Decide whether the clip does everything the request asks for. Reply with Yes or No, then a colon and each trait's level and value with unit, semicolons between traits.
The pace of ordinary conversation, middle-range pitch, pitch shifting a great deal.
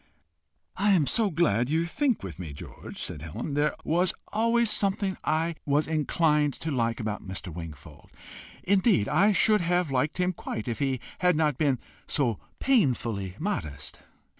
Yes: average, 160 wpm; medium, 150 Hz; wide, 8.0 semitones